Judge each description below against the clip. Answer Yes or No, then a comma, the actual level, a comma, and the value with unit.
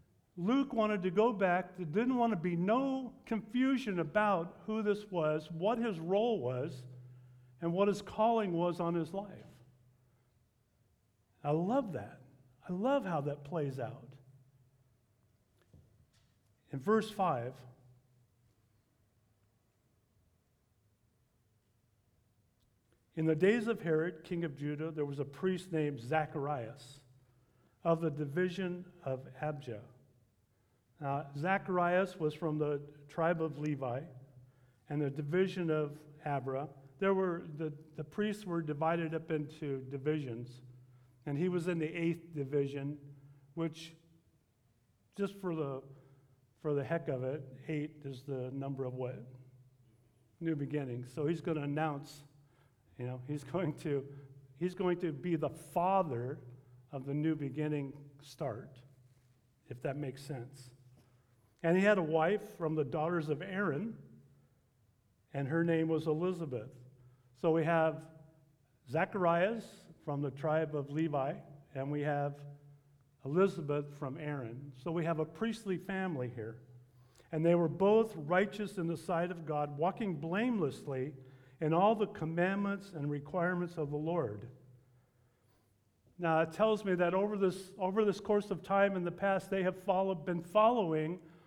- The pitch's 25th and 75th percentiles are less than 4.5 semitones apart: No, wide, 5.5 semitones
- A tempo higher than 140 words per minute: No, slow, 135 wpm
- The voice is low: No, medium, 150 Hz